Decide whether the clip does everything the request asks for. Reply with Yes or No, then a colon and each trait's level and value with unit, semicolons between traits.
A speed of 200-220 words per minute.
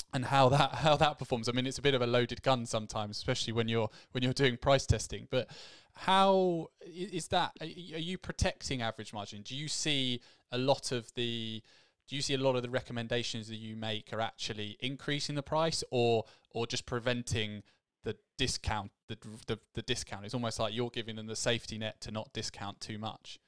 Yes: fast, 205 wpm